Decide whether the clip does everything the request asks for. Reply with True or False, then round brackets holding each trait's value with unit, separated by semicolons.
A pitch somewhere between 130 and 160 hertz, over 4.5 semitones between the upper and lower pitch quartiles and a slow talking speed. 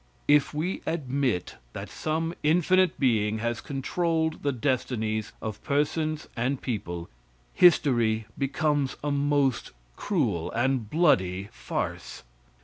True (135 Hz; 5.6 semitones; 110 wpm)